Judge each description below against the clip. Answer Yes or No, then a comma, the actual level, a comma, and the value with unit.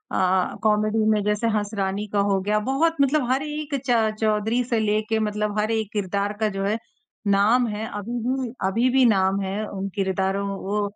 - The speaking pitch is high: Yes, high, 210 Hz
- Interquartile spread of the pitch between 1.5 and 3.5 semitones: Yes, narrow, 2.6 semitones